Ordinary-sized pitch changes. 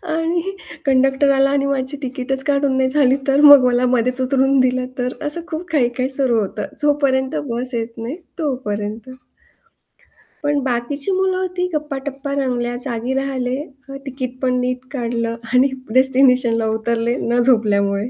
No: narrow, 2.3 semitones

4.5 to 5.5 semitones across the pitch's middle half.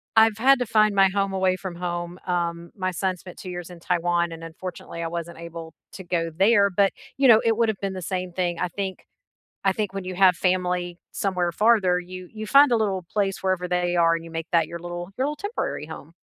No: narrow, 2.5 semitones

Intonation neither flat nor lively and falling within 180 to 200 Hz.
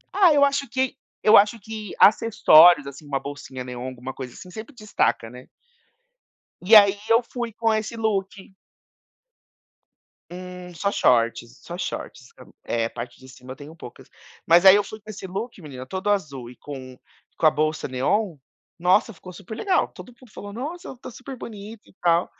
No: wide, 8.0 semitones; high, 190 Hz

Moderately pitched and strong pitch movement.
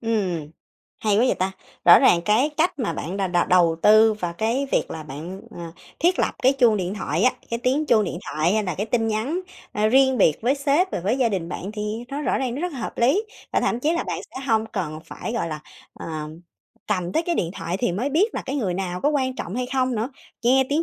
No: high, 220 Hz; wide, 6.4 semitones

